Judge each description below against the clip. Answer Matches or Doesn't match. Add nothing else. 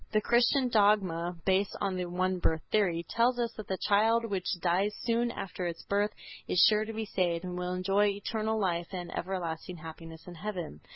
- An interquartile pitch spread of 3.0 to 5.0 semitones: Matches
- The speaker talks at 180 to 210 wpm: Matches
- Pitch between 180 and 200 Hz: Matches